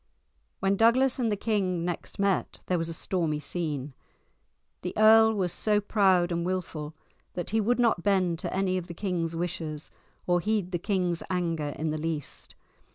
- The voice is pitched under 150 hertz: No, medium, 180 Hz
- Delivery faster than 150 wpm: Yes, average, 175 wpm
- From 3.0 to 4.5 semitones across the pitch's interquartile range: Yes, average, 3.5 semitones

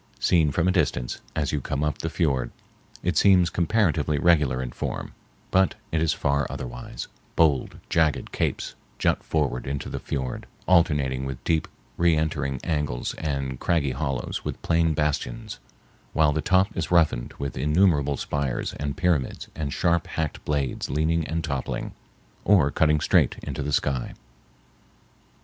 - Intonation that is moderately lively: Yes, average, 3.2 semitones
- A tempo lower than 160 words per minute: Yes, average, 150 wpm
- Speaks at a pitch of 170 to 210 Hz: No, very low, 75 Hz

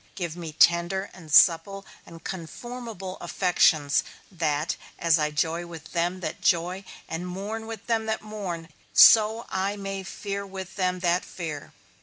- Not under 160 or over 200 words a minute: No, average, 150 wpm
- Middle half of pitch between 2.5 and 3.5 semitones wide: Yes, average, 3.0 semitones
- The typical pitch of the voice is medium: Yes, medium, 180 Hz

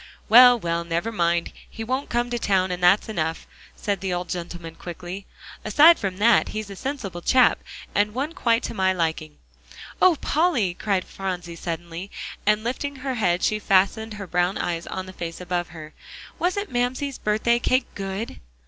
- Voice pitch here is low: No, high, 195 Hz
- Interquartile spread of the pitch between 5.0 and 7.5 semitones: Yes, average, 5.3 semitones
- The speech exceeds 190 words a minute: No, average, 175 wpm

